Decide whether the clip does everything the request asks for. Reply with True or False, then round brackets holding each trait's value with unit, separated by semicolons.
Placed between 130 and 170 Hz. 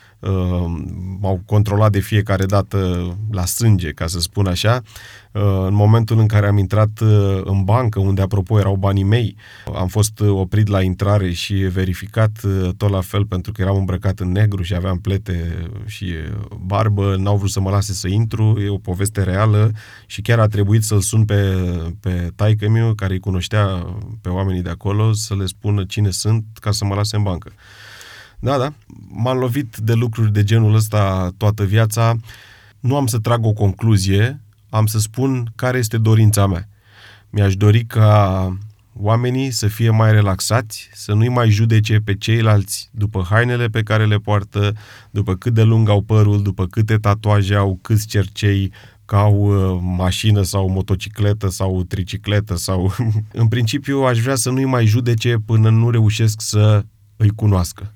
False (105 Hz)